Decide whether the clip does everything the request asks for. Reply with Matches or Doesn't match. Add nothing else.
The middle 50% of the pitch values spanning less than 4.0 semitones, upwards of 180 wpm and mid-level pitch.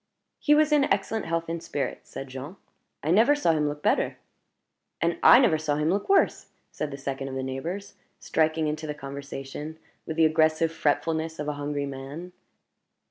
Matches